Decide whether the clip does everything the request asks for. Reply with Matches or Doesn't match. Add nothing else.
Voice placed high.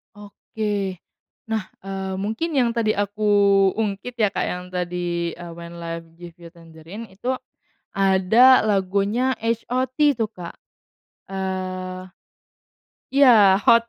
Matches